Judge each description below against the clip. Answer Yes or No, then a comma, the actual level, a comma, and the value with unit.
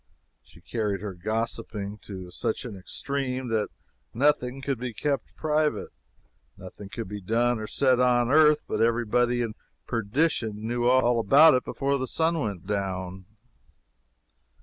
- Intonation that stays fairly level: No, average, 3.9 semitones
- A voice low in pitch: Yes, low, 120 Hz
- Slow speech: No, average, 150 wpm